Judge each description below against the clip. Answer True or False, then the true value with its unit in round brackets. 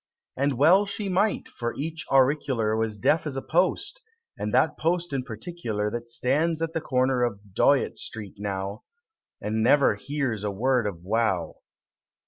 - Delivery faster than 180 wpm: False (165 wpm)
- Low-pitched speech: True (130 Hz)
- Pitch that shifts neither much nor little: False (6.4 semitones)